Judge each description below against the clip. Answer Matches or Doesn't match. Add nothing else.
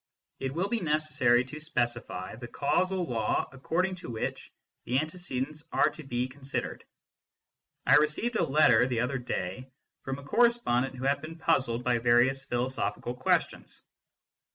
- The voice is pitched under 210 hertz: Matches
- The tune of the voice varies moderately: Matches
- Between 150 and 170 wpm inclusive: Matches